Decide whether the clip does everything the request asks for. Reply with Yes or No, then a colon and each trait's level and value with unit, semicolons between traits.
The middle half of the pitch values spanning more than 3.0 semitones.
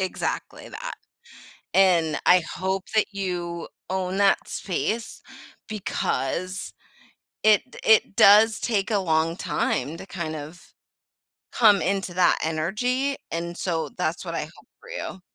Yes: average, 3.6 semitones